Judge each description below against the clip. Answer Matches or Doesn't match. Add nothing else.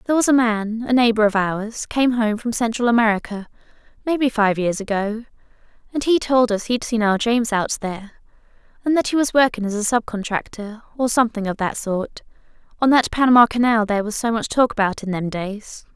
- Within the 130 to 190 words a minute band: Doesn't match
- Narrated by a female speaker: Matches